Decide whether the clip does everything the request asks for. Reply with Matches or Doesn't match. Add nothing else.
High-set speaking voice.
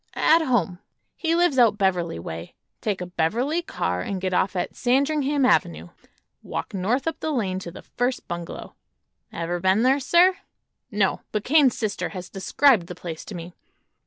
Matches